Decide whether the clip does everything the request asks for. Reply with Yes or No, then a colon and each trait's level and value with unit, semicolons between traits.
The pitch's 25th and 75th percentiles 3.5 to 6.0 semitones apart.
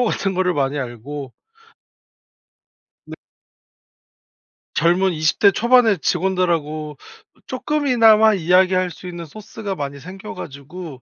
Yes: average, 5.1 semitones